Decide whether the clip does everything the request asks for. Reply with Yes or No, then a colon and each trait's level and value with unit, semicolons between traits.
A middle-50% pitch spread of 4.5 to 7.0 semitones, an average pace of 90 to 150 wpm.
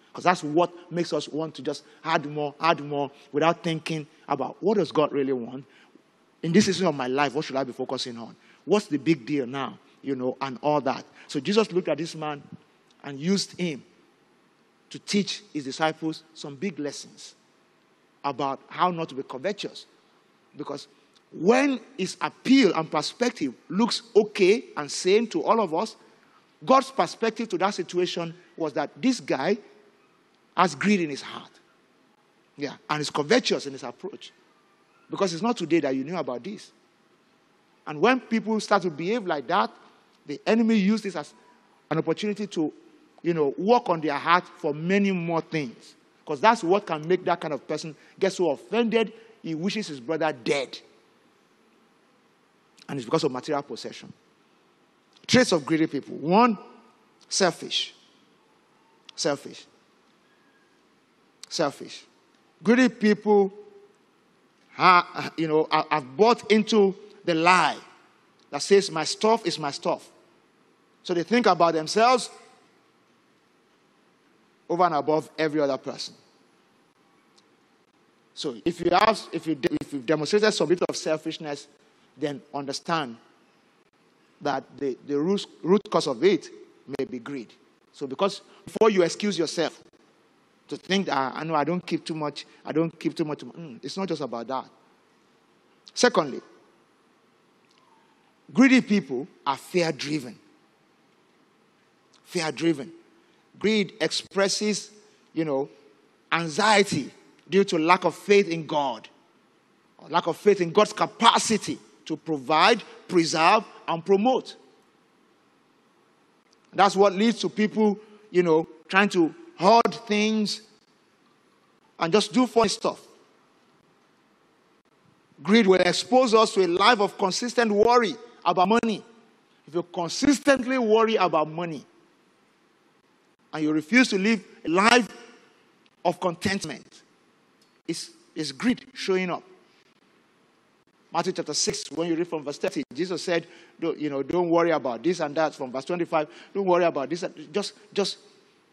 Yes: average, 5.3 semitones; average, 145 wpm